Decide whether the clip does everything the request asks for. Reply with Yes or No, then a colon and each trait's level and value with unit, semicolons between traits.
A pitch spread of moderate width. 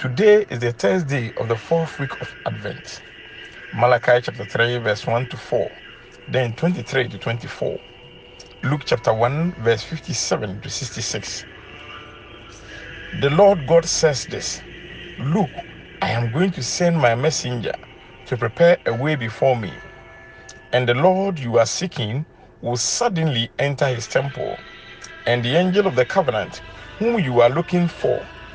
No: wide, 5.9 semitones